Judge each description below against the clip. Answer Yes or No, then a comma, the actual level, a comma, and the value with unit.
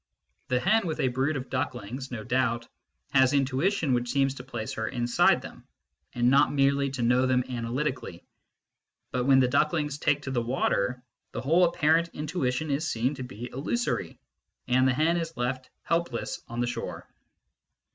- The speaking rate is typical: Yes, average, 170 wpm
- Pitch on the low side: Yes, low, 130 Hz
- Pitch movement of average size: Yes, average, 3.3 semitones